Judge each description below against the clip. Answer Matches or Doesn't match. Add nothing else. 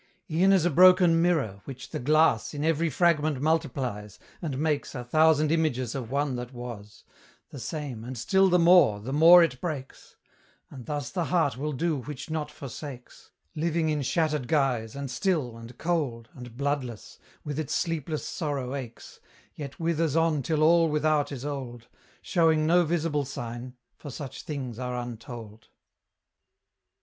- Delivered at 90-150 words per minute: Doesn't match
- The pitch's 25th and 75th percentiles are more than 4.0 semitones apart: Matches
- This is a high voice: Doesn't match